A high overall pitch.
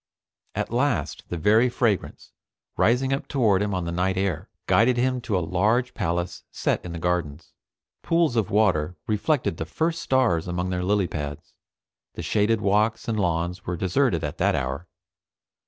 No: low, 100 Hz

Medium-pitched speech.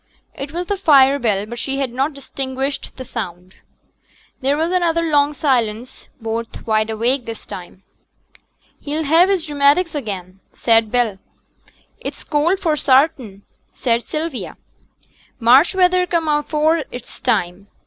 No: very high, 270 Hz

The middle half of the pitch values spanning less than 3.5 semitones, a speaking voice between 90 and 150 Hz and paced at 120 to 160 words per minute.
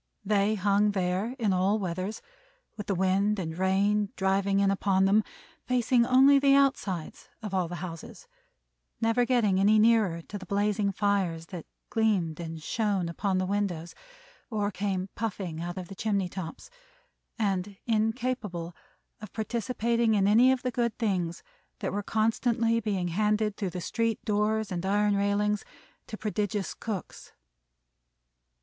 No: average, 2.7 semitones; high, 205 Hz; average, 150 wpm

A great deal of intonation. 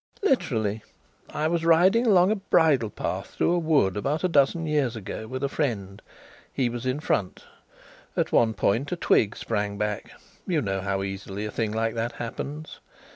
Yes: wide, 7.2 semitones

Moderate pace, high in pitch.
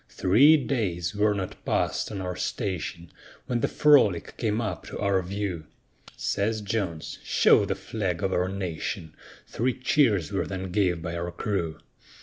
No: average, 155 wpm; very low, 95 Hz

